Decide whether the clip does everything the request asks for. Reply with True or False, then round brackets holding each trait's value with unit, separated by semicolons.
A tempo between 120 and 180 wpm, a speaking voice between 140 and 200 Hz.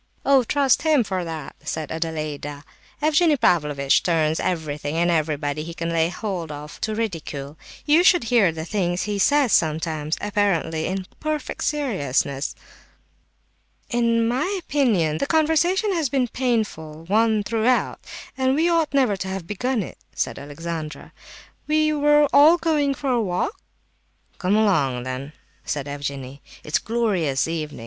True (150 wpm; 190 Hz)